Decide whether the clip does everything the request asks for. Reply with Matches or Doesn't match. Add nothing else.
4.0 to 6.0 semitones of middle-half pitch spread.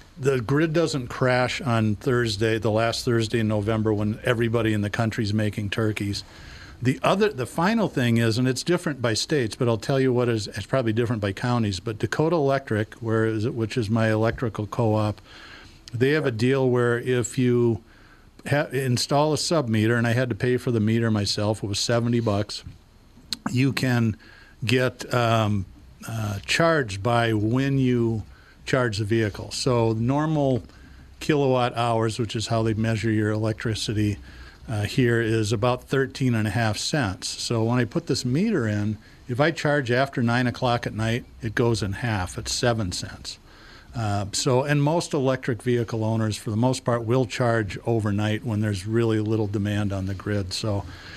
Doesn't match